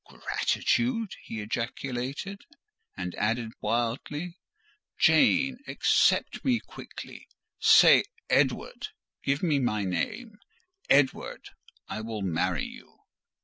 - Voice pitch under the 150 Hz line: Yes, medium, 140 Hz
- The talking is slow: Yes, slow, 75 wpm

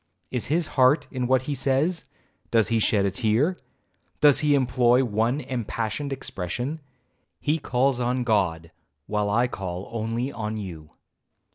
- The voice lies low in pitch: Yes, low, 120 Hz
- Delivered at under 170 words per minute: Yes, average, 140 wpm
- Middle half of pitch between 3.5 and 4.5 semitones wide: Yes, average, 4.1 semitones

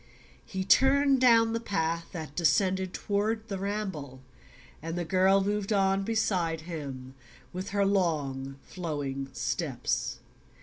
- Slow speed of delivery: Yes, slow, 125 wpm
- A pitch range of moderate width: Yes, average, 4.2 semitones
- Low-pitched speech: No, high, 190 Hz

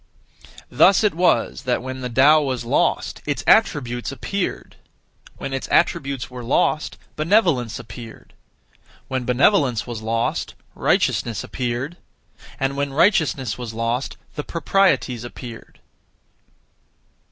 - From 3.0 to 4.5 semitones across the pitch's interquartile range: Yes, average, 3.9 semitones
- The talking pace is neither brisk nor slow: No, slow, 115 wpm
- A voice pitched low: Yes, low, 130 Hz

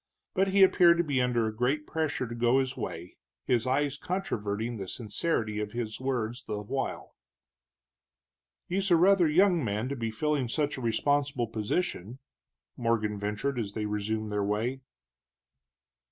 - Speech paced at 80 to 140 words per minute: No, average, 155 wpm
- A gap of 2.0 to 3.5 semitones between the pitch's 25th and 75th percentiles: No, average, 5.3 semitones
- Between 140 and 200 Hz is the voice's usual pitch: No, low, 120 Hz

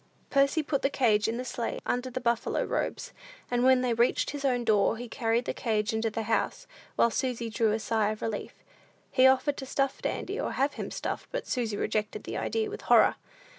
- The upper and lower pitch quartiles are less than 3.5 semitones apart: Yes, average, 2.9 semitones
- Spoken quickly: Yes, fast, 210 wpm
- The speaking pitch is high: Yes, high, 240 Hz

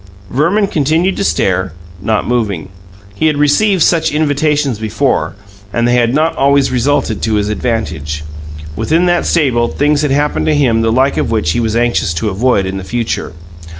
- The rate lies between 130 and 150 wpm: No, average, 180 wpm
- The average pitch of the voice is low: Yes, low, 125 Hz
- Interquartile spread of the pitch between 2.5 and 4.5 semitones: No, average, 5.3 semitones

